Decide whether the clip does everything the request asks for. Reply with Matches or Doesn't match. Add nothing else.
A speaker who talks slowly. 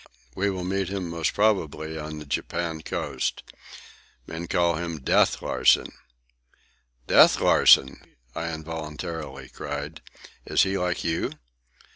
Matches